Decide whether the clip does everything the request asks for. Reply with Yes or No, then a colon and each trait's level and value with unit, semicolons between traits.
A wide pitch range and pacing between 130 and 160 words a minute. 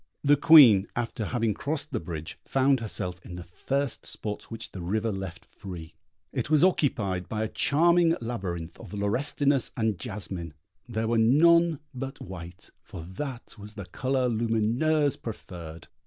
Yes: wide, 6.6 semitones; average, 155 wpm